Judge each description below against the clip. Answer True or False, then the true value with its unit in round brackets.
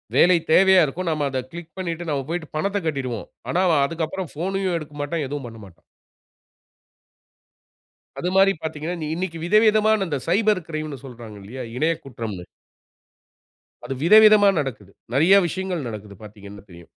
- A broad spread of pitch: True (5.9 semitones)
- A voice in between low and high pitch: True (160 Hz)